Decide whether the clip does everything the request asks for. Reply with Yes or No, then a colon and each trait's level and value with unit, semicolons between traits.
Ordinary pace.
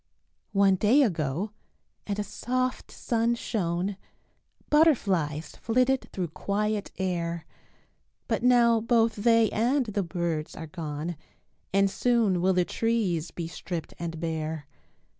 No: slow, 120 wpm